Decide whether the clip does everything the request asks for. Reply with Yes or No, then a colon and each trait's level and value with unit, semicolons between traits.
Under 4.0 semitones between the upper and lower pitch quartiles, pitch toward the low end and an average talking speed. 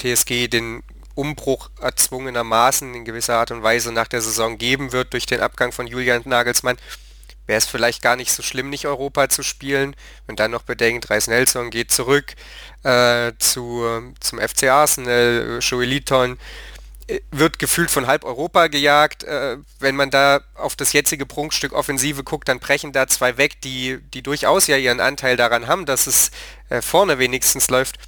Yes: average, 2.8 semitones; low, 130 Hz; average, 170 wpm